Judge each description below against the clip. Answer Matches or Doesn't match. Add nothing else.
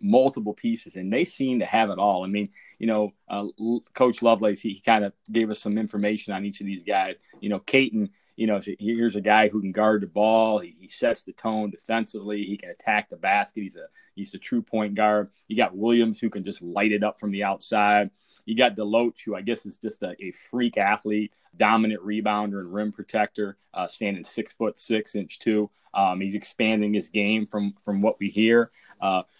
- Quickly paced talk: Matches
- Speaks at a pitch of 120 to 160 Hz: Doesn't match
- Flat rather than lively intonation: Matches